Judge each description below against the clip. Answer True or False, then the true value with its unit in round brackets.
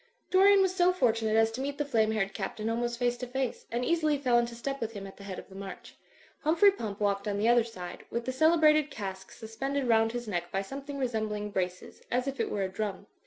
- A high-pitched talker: True (235 Hz)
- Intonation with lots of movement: False (4.8 semitones)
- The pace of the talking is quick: True (250 wpm)